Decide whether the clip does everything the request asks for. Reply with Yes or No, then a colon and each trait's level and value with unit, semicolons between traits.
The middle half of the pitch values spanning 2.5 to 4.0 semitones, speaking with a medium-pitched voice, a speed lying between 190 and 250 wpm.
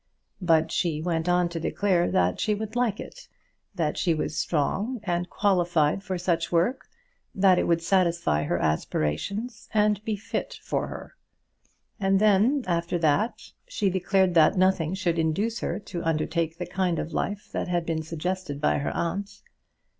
No: average, 3.5 semitones; medium, 180 Hz; average, 165 wpm